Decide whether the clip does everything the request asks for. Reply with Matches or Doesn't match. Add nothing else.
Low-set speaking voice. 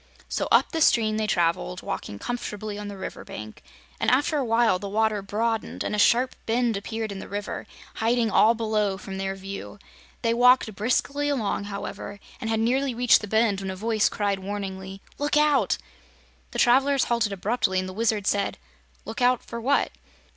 Doesn't match